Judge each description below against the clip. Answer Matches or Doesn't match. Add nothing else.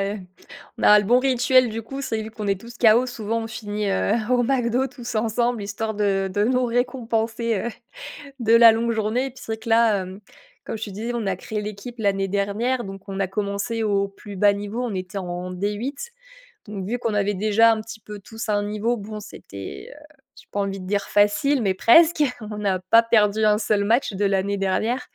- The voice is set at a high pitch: Matches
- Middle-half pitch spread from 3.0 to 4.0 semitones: Doesn't match